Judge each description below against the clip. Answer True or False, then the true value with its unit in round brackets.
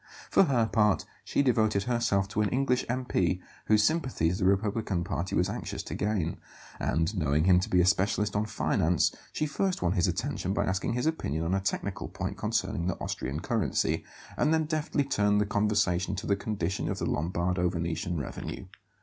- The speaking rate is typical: True (185 wpm)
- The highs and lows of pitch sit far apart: False (4.1 semitones)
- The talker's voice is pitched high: False (100 Hz)